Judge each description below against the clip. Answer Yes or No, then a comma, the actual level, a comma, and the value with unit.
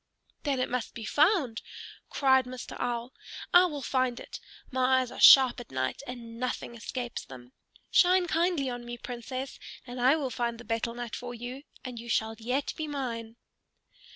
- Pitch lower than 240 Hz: No, very high, 250 Hz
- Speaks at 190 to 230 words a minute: No, average, 180 wpm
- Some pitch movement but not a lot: No, narrow, 2.2 semitones